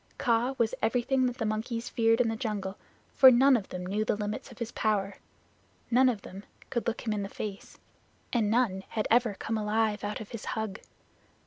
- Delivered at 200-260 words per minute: Yes, fast, 205 wpm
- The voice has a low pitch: No, high, 220 Hz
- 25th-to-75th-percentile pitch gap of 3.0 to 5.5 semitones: No, narrow, 2.4 semitones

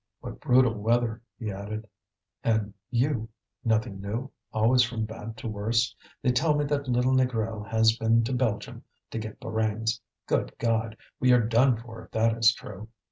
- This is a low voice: Yes, low, 115 Hz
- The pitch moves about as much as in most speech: No, narrow, 2.0 semitones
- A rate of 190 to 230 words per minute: No, average, 170 wpm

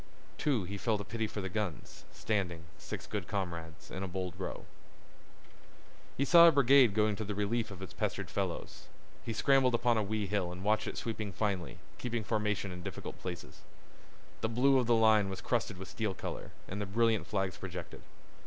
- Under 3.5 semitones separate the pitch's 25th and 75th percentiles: Yes, average, 3.1 semitones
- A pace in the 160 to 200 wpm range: Yes, average, 190 wpm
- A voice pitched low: Yes, low, 105 Hz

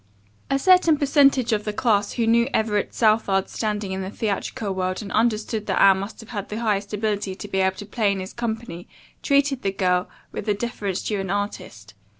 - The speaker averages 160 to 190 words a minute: No, fast, 205 wpm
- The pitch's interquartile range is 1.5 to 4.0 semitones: Yes, average, 3.0 semitones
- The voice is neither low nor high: No, high, 210 Hz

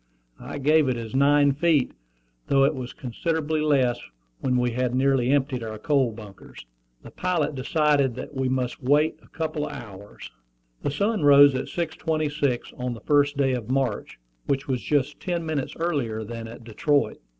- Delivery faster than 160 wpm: Yes, average, 170 wpm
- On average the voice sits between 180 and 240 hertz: No, low, 135 Hz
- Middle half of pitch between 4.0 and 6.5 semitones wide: No, average, 3.3 semitones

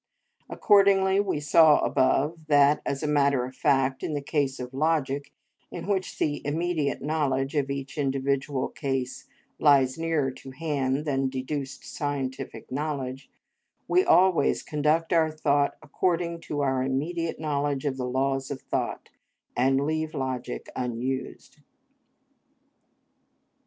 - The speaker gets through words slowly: Yes, slow, 130 wpm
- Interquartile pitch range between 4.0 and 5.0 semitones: No, average, 2.8 semitones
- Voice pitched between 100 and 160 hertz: Yes, medium, 140 Hz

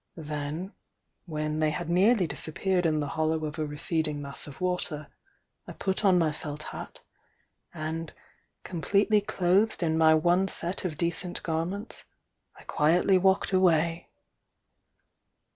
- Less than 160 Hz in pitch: No, medium, 165 Hz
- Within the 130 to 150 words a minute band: Yes, average, 140 wpm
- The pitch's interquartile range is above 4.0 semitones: No, average, 3.0 semitones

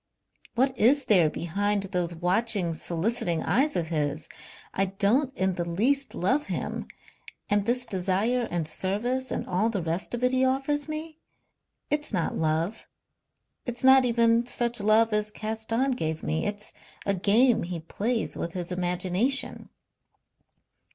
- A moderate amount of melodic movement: No, wide, 5.8 semitones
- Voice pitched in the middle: No, high, 210 Hz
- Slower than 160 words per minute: Yes, average, 145 wpm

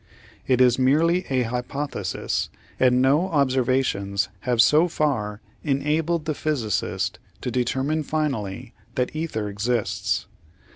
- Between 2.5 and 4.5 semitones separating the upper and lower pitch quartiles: Yes, average, 4.1 semitones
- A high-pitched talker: No, low, 130 Hz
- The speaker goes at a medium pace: No, slow, 110 wpm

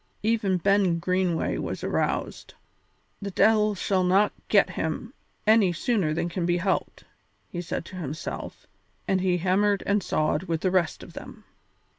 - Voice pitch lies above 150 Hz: Yes, medium, 185 Hz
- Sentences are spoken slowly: No, average, 155 wpm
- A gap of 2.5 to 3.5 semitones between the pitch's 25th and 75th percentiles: Yes, average, 2.8 semitones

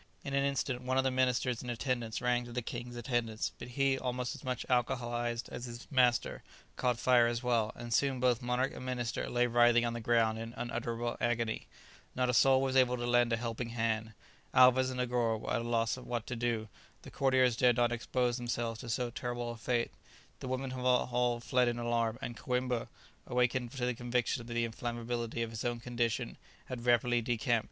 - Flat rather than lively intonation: Yes, narrow, 1.1 semitones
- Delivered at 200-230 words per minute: Yes, fast, 205 wpm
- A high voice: No, low, 120 Hz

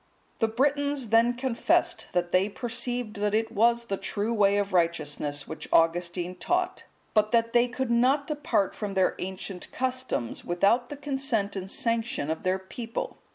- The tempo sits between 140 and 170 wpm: Yes, average, 160 wpm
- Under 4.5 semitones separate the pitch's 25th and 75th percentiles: No, average, 4.8 semitones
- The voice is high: Yes, high, 225 Hz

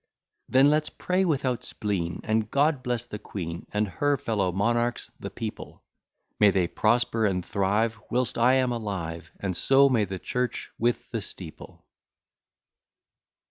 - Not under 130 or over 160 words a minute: Yes, average, 145 wpm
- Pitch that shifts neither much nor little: Yes, average, 4.3 semitones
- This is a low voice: Yes, low, 115 Hz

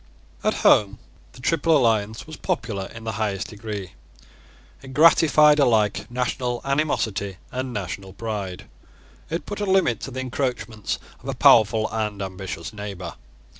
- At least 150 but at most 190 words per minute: No, average, 140 wpm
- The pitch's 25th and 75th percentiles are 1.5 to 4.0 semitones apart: No, average, 4.5 semitones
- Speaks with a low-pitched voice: Yes, low, 110 Hz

